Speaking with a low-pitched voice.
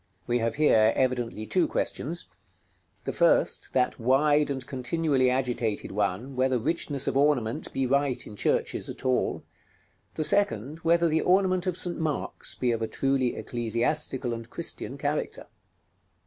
Yes: low, 130 Hz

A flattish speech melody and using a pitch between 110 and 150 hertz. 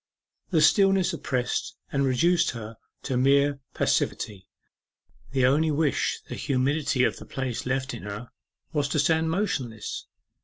No: average, 4.0 semitones; medium, 140 Hz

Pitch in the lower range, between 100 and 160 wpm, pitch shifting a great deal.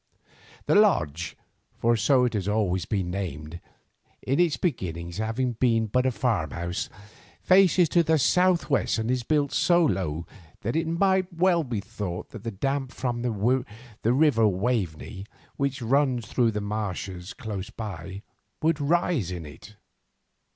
Yes: low, 115 Hz; average, 150 wpm; wide, 6.8 semitones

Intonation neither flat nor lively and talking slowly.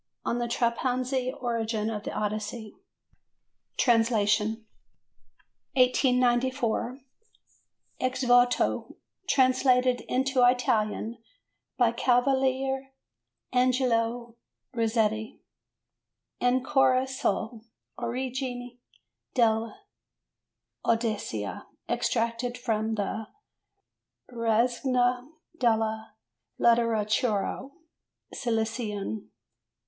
No: narrow, 2.3 semitones; slow, 60 wpm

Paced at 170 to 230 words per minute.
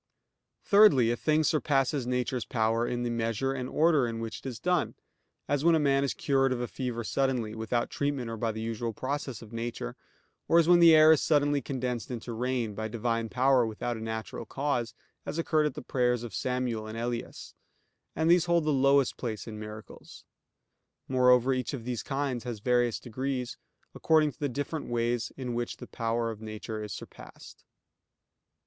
Yes: average, 185 wpm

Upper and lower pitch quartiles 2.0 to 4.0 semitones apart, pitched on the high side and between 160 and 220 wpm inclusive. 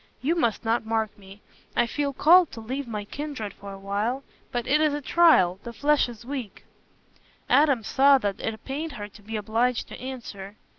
No: average, 5.1 semitones; high, 235 Hz; average, 190 wpm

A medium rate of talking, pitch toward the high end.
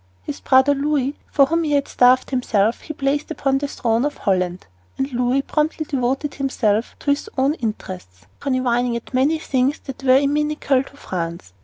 Yes: average, 175 wpm; very high, 270 Hz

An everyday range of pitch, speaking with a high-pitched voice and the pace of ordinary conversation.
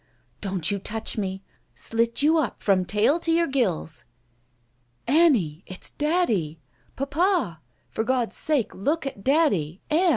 No: wide, 8.3 semitones; high, 230 Hz; average, 150 wpm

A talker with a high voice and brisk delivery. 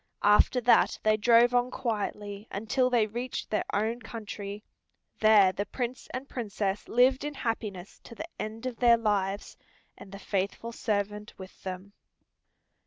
No: high, 215 Hz; average, 150 wpm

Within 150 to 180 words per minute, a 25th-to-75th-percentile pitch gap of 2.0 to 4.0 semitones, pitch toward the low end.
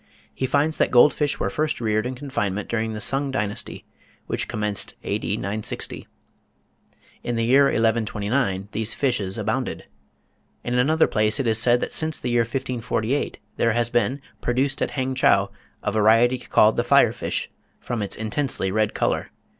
Yes: average, 160 wpm; average, 3.6 semitones; low, 120 Hz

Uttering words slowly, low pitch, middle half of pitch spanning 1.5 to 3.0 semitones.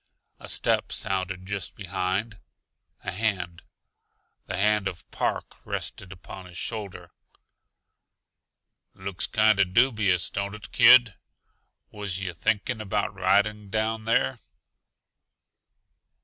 Yes: slow, 105 wpm; low, 100 Hz; narrow, 2.6 semitones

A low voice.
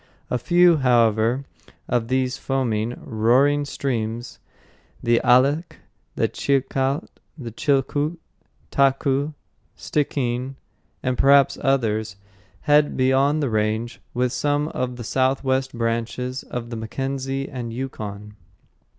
Yes: low, 130 Hz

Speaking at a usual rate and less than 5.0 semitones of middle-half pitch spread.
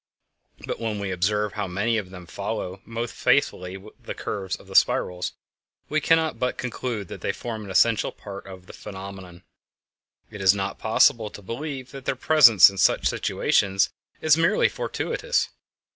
Yes: average, 165 wpm; average, 4.1 semitones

